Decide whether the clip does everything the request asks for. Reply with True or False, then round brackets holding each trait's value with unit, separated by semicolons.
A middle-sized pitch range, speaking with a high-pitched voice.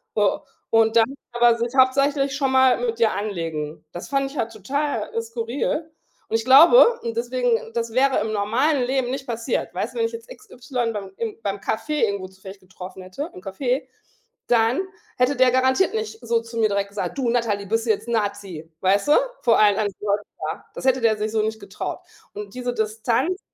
True (4.4 semitones; 230 Hz)